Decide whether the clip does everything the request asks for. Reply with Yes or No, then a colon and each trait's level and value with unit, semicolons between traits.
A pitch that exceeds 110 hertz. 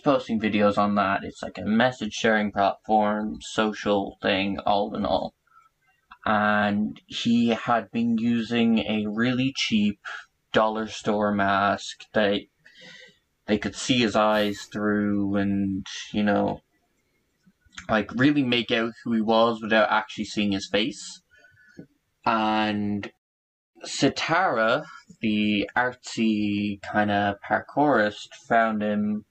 No: low, 105 Hz